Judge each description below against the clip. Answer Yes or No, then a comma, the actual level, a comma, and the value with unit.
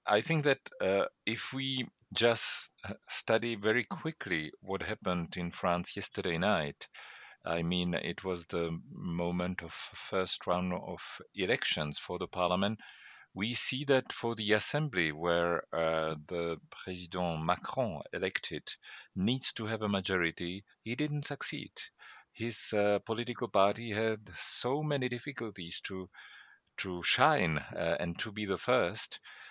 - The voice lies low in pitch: Yes, low, 100 Hz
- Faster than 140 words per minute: No, slow, 135 wpm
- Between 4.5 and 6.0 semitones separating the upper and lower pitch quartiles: Yes, average, 4.9 semitones